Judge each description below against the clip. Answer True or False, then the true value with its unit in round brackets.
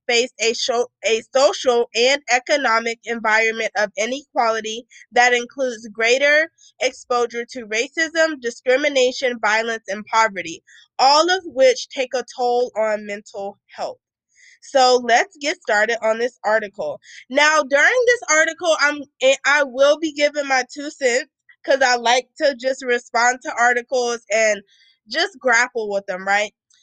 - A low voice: False (250 Hz)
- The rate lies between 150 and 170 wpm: False (140 wpm)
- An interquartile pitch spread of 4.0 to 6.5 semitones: True (4.4 semitones)